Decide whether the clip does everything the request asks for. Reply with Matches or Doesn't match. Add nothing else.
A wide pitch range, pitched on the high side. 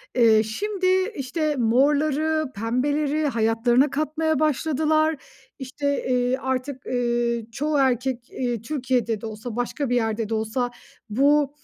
Doesn't match